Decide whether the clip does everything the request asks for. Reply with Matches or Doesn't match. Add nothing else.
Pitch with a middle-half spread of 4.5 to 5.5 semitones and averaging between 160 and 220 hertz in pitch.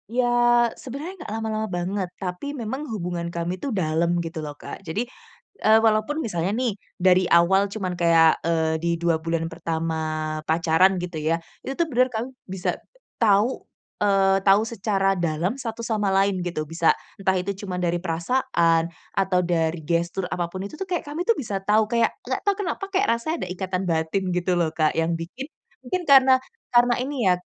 Matches